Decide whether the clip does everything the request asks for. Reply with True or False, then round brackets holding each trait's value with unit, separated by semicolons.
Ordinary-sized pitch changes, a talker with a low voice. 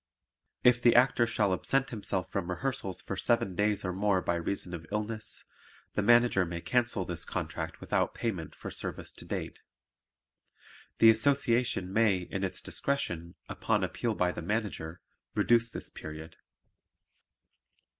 True (4.6 semitones; 100 Hz)